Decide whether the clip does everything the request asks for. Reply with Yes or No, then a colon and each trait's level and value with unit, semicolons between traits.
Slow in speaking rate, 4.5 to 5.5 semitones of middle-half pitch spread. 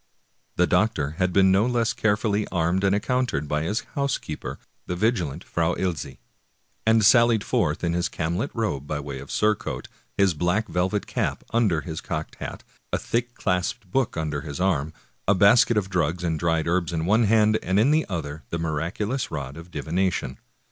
No: average, 185 wpm; average, 5.0 semitones